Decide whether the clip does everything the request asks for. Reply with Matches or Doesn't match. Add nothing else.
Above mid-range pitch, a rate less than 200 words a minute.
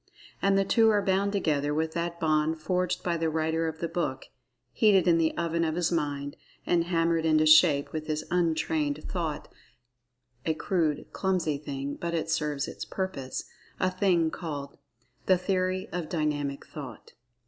Doesn't match